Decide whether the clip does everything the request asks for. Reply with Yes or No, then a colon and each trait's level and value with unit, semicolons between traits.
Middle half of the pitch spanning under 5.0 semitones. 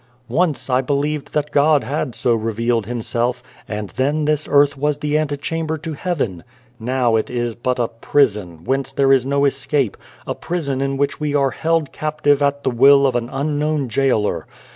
Yes: average, 3.3 semitones